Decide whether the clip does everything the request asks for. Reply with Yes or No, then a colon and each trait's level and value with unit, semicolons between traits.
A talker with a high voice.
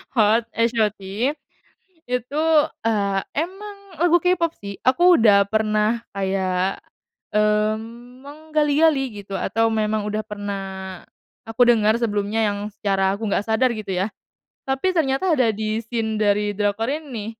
Yes: high, 220 Hz